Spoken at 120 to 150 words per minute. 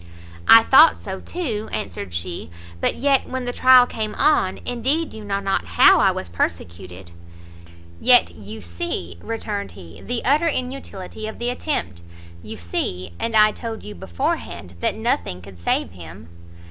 No: average, 160 wpm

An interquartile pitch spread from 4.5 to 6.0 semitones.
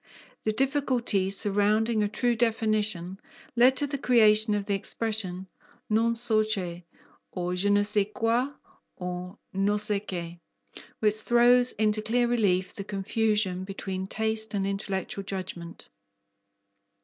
No: average, 2.8 semitones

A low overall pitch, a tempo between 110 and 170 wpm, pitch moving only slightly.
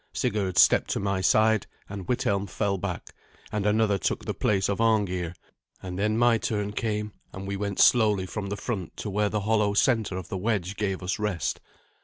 No: low, 100 Hz; average, 195 wpm; narrow, 1.9 semitones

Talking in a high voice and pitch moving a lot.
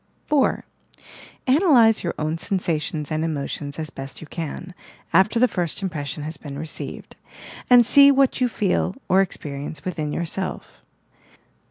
No: medium, 170 Hz; wide, 6.5 semitones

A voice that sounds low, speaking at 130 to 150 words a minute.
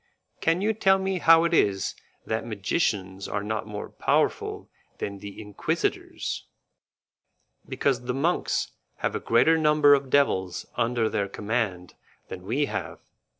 Yes: low, 115 Hz; average, 140 wpm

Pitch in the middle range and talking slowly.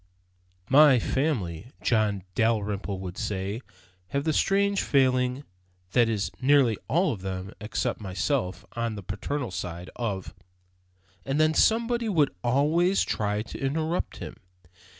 No: low, 115 Hz; slow, 130 wpm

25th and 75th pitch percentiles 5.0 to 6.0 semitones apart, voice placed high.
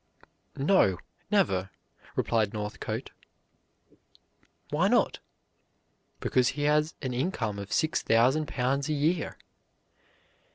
No: wide, 5.4 semitones; low, 135 Hz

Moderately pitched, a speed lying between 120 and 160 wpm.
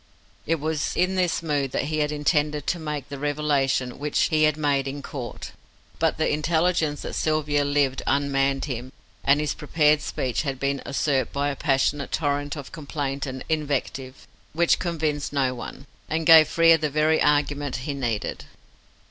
No: medium, 145 Hz; average, 170 wpm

